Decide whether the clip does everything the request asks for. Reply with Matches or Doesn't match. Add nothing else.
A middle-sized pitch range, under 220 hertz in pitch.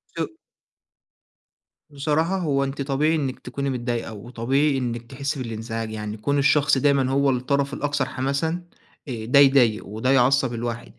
Matches